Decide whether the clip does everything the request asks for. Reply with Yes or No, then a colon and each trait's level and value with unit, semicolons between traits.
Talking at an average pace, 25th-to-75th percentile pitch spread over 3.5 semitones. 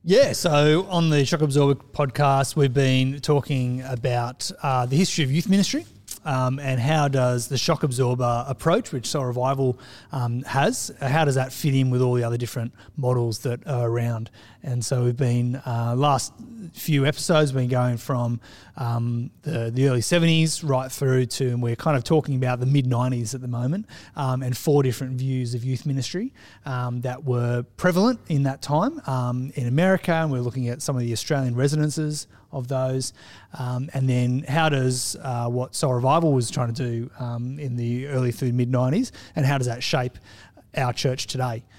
No: average, 190 wpm; average, 2.8 semitones